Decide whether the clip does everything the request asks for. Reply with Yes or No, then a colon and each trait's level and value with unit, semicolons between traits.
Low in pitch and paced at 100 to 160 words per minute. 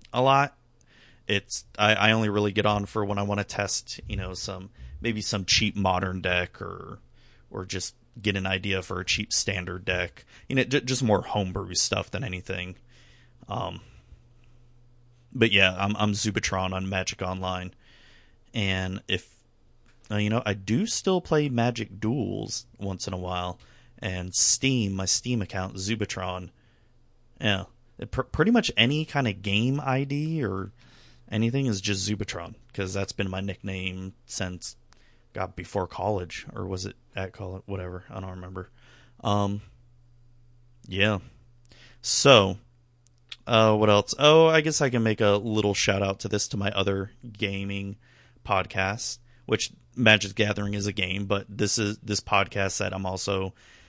Yes: low, 105 Hz; average, 155 wpm